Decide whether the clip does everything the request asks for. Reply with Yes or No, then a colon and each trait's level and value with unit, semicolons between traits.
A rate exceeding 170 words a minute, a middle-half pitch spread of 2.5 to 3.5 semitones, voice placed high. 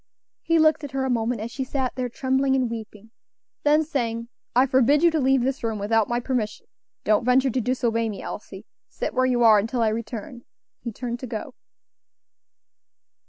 Yes: average, 190 wpm; average, 2.8 semitones; high, 245 Hz